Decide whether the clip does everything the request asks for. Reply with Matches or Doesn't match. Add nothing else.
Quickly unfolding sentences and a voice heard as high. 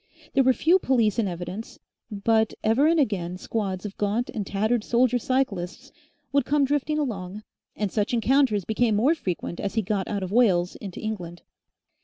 Doesn't match